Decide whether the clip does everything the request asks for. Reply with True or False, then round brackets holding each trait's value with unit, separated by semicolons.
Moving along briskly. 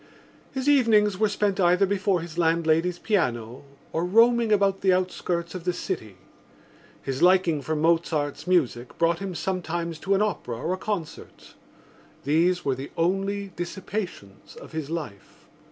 False (150 wpm)